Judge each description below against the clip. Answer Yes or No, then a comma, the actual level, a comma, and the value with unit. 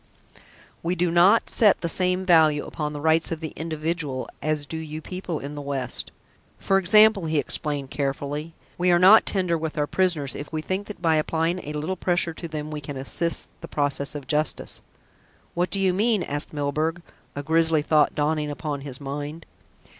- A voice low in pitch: No, medium, 160 Hz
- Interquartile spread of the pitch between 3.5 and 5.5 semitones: No, average, 3.1 semitones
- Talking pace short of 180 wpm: No, average, 190 wpm